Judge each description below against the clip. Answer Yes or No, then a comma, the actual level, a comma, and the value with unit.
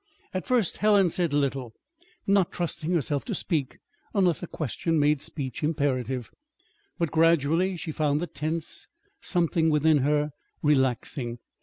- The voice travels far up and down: No, average, 3.3 semitones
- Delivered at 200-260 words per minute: No, slow, 135 wpm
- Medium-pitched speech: Yes, medium, 155 Hz